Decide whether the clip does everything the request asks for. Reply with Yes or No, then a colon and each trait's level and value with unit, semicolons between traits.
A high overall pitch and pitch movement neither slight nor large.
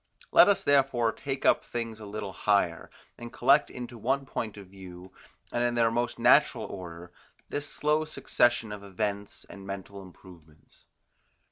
No: low, 110 Hz; average, 4.0 semitones